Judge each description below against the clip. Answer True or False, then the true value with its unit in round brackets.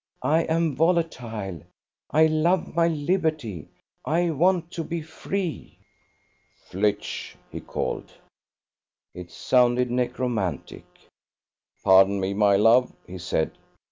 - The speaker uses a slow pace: True (110 wpm)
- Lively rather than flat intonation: True (8.4 semitones)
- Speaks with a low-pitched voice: True (130 Hz)